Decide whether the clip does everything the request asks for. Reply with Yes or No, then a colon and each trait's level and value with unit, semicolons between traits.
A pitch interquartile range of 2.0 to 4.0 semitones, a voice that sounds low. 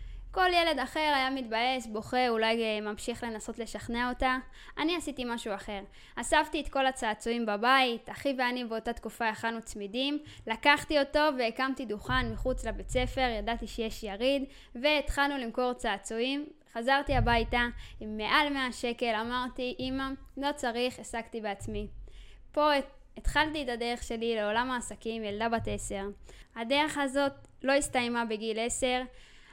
No: average, 3.2 semitones; high, 245 Hz